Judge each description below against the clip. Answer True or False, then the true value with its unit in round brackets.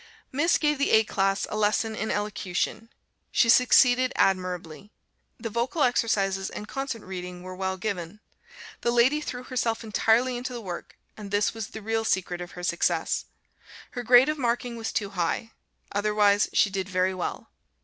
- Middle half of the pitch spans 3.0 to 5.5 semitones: True (4.0 semitones)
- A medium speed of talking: True (170 wpm)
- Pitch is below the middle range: False (215 Hz)